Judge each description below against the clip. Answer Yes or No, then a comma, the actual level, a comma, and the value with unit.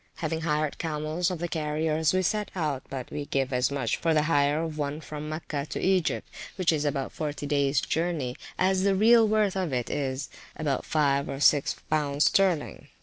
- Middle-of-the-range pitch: Yes, medium, 155 Hz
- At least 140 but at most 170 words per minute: No, average, 200 wpm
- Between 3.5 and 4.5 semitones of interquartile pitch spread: No, average, 3.1 semitones